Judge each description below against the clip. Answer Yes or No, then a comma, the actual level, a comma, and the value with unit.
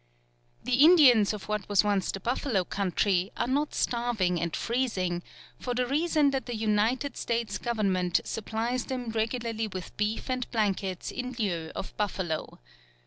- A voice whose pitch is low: No, high, 220 Hz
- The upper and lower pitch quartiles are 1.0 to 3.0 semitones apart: No, average, 4.3 semitones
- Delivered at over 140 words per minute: Yes, average, 150 wpm